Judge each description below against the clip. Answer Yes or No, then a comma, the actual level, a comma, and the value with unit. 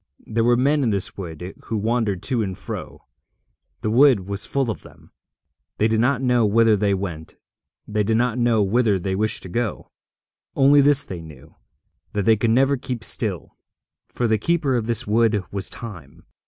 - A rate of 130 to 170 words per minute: No, average, 185 wpm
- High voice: No, low, 110 Hz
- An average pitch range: Yes, average, 3.6 semitones